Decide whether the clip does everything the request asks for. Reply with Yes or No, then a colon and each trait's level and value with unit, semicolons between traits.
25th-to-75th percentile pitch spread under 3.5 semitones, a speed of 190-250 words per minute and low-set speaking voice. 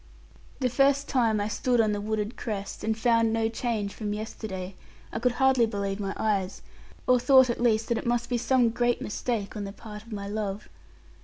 No: average, 2.7 semitones; fast, 205 wpm; high, 225 Hz